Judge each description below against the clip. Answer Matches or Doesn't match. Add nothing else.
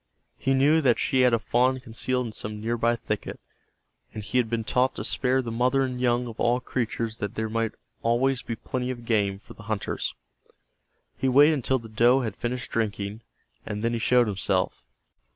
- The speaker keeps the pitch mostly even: Matches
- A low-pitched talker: Matches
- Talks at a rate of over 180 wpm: Matches